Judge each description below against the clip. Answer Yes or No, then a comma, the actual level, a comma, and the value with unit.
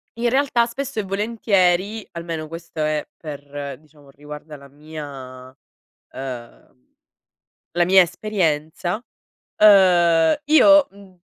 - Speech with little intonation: No, wide, 5.6 semitones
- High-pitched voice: No, medium, 170 Hz